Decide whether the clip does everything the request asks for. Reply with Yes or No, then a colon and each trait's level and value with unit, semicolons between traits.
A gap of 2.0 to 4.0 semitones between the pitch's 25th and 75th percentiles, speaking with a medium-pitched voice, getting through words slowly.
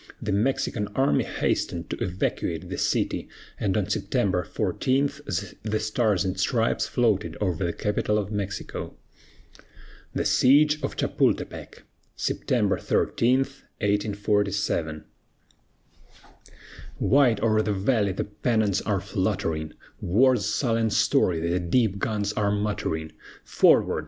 No: average, 3.0 semitones; low, 105 Hz; slow, 115 wpm